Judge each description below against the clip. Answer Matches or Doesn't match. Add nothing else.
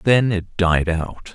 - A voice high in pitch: Doesn't match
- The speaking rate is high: Doesn't match